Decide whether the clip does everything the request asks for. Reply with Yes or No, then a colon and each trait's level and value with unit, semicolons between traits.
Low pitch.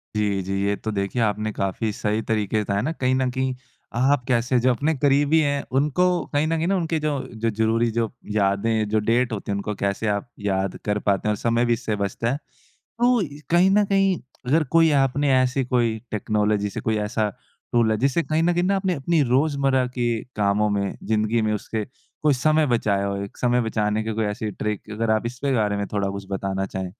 Yes: low, 115 Hz